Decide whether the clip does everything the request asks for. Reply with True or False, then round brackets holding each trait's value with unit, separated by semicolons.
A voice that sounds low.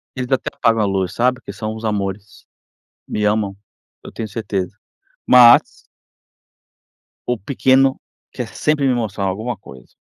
True (110 Hz)